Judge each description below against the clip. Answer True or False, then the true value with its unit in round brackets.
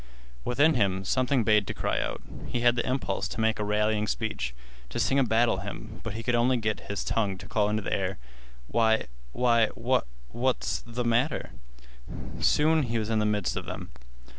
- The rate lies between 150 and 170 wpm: False (185 wpm)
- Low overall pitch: True (110 Hz)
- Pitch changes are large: False (2.7 semitones)